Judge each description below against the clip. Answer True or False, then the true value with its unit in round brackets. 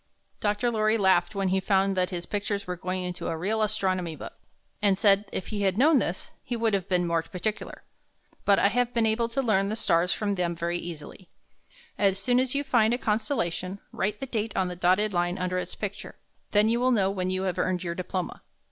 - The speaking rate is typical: False (220 wpm)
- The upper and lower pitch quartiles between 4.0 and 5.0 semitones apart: False (3.1 semitones)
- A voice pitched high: True (195 Hz)